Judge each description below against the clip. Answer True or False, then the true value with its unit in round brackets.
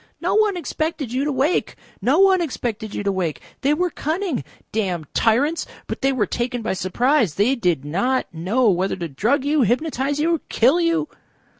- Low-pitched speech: False (255 Hz)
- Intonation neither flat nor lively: False (7.1 semitones)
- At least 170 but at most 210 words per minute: True (180 wpm)